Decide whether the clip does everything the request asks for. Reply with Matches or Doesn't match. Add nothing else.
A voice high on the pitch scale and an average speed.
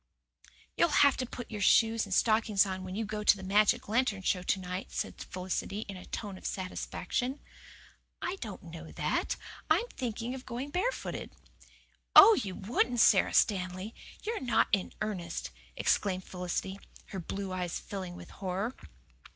Matches